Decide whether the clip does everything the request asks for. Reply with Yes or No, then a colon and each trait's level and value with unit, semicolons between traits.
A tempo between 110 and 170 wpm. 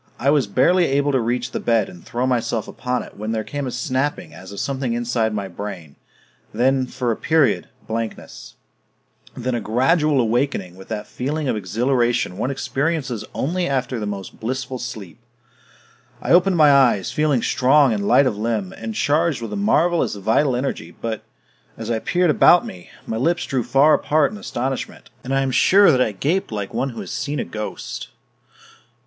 No: average, 185 wpm